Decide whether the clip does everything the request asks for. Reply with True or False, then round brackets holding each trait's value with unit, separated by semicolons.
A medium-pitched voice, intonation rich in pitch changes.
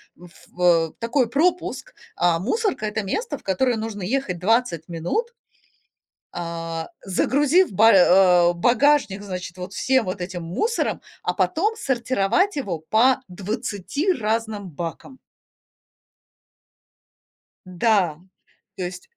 False (205 Hz; 6.7 semitones)